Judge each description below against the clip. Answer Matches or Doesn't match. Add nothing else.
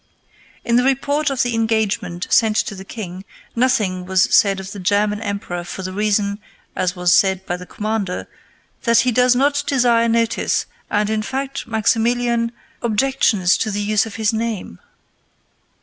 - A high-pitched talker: Matches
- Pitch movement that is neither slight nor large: Matches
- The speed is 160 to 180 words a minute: Matches